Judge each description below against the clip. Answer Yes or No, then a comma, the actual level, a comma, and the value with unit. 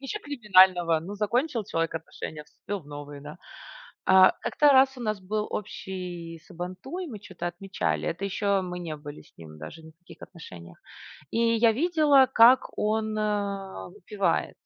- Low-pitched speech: No, high, 195 Hz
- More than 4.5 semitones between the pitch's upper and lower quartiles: Yes, average, 5.0 semitones